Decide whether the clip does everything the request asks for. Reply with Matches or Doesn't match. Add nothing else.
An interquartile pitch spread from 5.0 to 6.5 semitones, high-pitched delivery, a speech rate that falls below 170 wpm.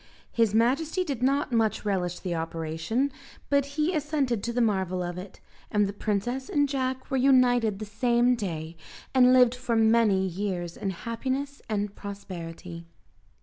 Matches